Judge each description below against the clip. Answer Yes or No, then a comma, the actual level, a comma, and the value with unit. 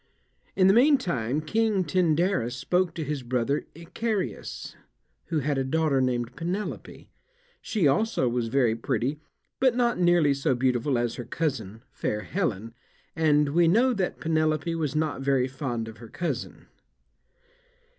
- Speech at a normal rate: Yes, average, 145 wpm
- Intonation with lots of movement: Yes, wide, 5.7 semitones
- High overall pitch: No, medium, 150 Hz